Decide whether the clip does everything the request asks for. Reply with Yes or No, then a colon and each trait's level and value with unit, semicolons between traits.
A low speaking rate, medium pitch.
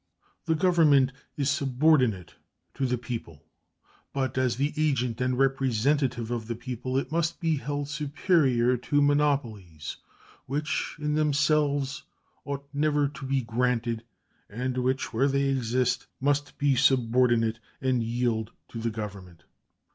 No: slow, 130 wpm; low, 130 Hz